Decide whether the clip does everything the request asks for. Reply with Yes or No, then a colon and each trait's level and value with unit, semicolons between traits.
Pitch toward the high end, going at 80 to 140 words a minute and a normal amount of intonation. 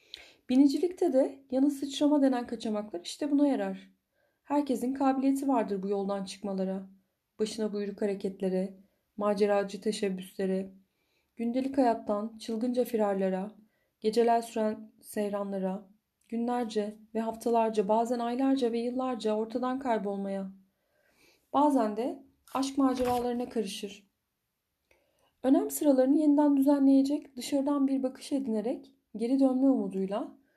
Yes: high, 230 Hz; average, 100 wpm; average, 4.7 semitones